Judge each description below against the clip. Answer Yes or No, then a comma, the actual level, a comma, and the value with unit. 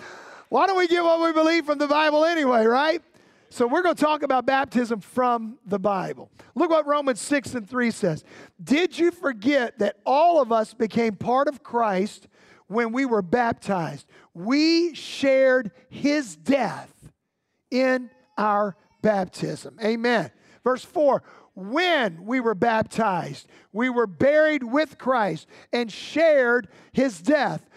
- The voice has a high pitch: Yes, very high, 255 Hz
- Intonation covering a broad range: No, average, 5.0 semitones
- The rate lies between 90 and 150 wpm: Yes, average, 145 wpm